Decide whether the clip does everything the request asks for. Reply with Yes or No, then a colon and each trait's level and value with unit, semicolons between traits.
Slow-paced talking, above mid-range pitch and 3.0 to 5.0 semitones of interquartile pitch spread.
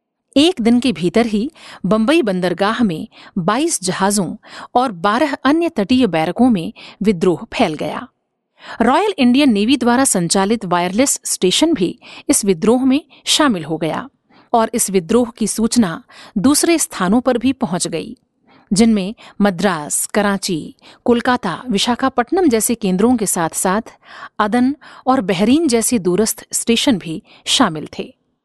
No: average, 135 wpm; high, 230 Hz; average, 4.5 semitones